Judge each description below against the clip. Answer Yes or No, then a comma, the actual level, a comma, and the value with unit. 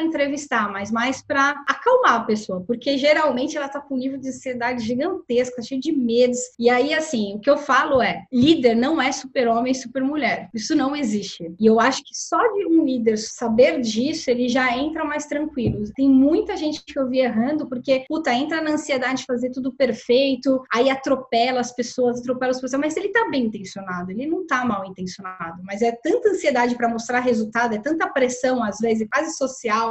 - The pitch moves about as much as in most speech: Yes, average, 3.3 semitones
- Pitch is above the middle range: Yes, very high, 255 Hz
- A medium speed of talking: No, fast, 205 wpm